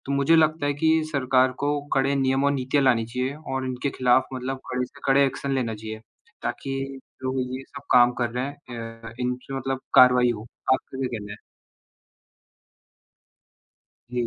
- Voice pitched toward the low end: Yes, low, 130 Hz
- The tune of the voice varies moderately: No, narrow, 1.8 semitones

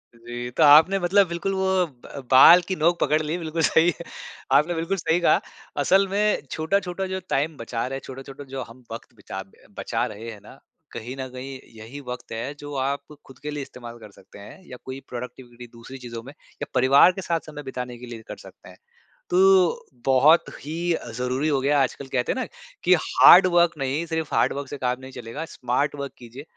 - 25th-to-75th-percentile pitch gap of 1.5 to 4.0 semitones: No, average, 4.9 semitones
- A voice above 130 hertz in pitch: Yes, medium, 140 Hz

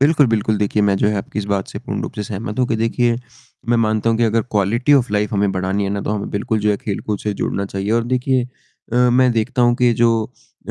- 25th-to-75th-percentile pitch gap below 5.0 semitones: Yes, average, 2.7 semitones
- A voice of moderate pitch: No, low, 110 Hz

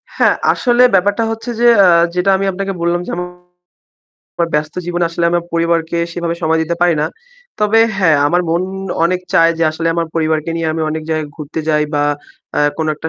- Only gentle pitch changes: Yes, narrow, 1.8 semitones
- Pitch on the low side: No, medium, 170 Hz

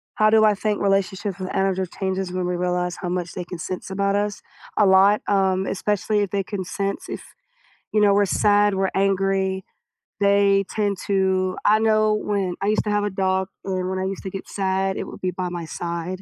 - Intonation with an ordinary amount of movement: No, narrow, 1.5 semitones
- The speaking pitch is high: Yes, high, 195 Hz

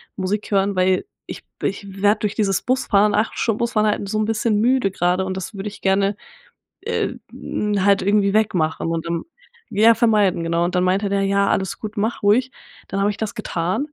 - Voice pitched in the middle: No, high, 200 Hz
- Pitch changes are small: Yes, narrow, 2.1 semitones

